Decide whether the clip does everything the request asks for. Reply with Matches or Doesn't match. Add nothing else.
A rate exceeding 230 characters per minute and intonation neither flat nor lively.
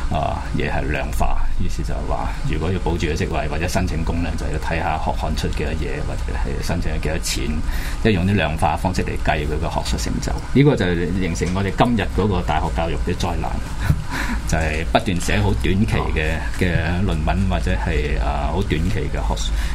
Matches